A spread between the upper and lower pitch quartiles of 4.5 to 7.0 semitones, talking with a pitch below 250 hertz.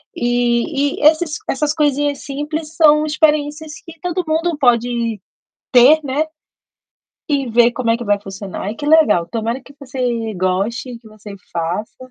No: average, 4.8 semitones; very high, 260 Hz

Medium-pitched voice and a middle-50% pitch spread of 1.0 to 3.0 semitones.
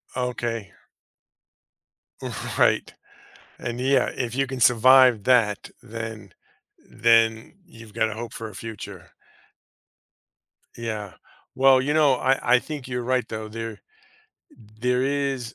No: low, 120 Hz; narrow, 2.5 semitones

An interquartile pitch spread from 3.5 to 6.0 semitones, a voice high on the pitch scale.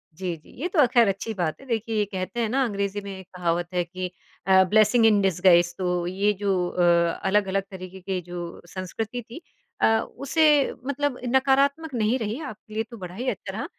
Yes: average, 4.5 semitones; high, 205 Hz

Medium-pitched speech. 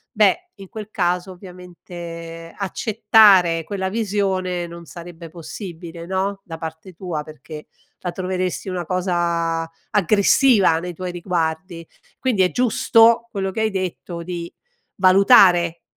Yes: medium, 180 Hz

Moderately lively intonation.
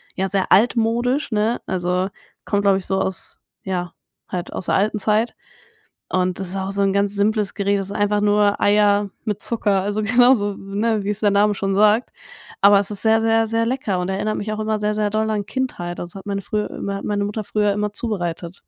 No: narrow, 1.7 semitones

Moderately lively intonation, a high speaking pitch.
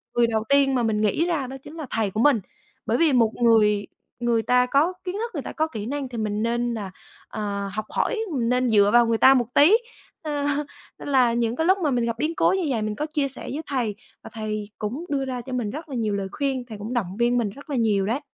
Yes: average, 4.4 semitones; high, 240 Hz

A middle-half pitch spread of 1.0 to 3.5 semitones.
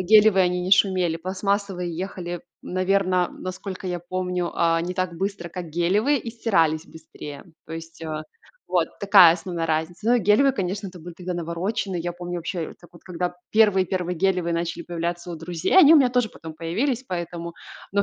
Yes: narrow, 2.5 semitones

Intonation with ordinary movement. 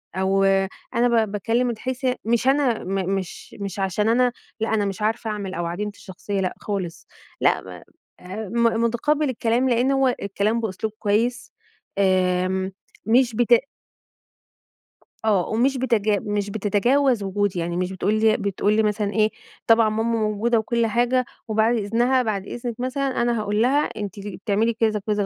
Yes: average, 3.0 semitones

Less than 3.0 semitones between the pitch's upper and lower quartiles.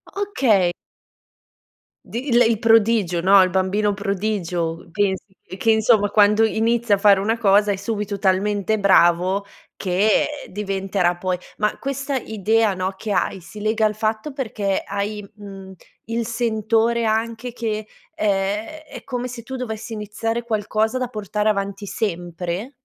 Yes: narrow, 2.5 semitones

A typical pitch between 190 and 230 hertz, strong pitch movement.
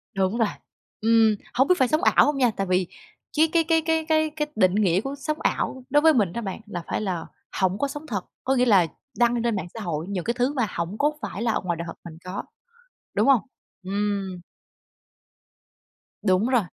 Yes: high, 225 Hz; wide, 6.5 semitones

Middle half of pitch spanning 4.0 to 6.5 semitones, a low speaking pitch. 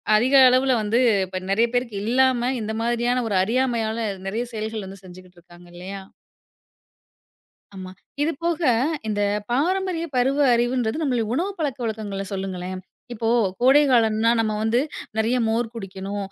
No: average, 4.3 semitones; high, 225 Hz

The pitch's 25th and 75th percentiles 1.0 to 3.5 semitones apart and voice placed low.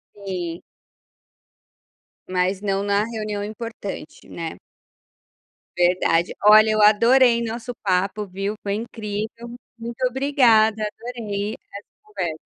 No: average, 2.9 semitones; high, 210 Hz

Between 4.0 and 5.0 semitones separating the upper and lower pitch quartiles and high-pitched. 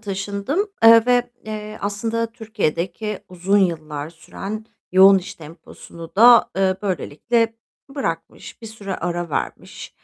Yes: average, 4.5 semitones; high, 200 Hz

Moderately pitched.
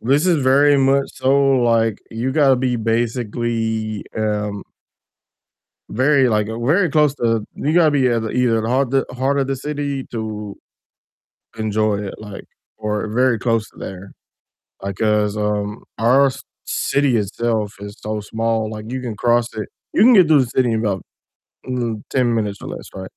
No: low, 115 Hz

